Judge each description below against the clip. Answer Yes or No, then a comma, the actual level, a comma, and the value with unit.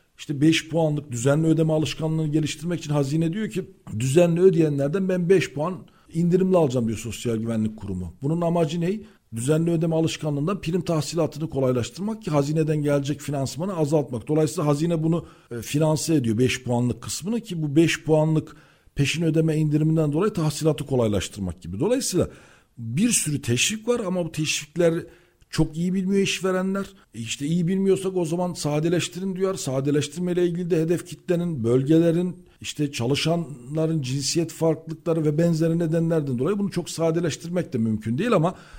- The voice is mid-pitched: Yes, medium, 160 Hz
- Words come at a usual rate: No, fast, 150 wpm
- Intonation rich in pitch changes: No, average, 3.4 semitones